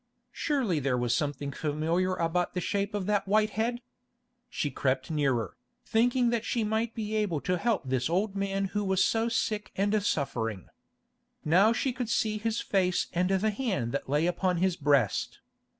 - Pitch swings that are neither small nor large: No, wide, 6.0 semitones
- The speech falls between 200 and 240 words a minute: No, average, 175 wpm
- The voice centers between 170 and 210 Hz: Yes, high, 190 Hz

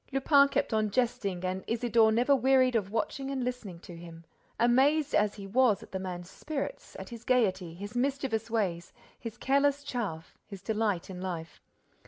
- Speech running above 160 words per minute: Yes, average, 175 wpm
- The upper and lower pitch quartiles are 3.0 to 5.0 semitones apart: No, wide, 5.5 semitones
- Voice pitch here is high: Yes, high, 225 Hz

